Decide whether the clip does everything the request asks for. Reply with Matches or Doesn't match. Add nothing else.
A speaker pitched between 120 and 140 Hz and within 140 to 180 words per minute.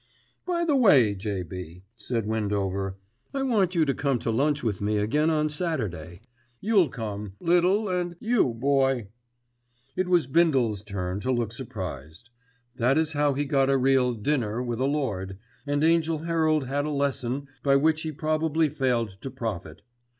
Matches